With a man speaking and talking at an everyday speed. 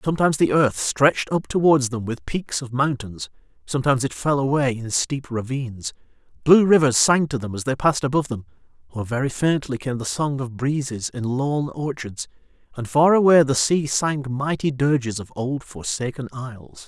Yes: male; average, 180 wpm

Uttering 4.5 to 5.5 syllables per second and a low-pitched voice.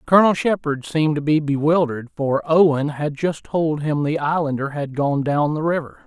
No: 5.2 syllables/s; medium, 150 Hz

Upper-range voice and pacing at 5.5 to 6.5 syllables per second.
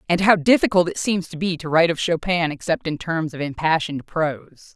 No: medium, 165 Hz; 5.7 syllables/s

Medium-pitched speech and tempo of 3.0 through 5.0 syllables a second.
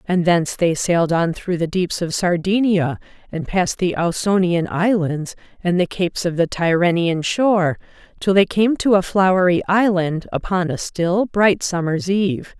Yes: medium, 180 Hz; 4.6 syllables/s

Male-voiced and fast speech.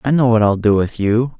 Yes: male; fast, 300 wpm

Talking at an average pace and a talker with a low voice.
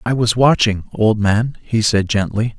Yes: average, 185 wpm; low, 110 Hz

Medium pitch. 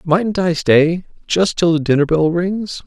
Yes: medium, 170 Hz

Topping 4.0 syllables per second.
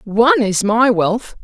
No: 3.9 syllables/s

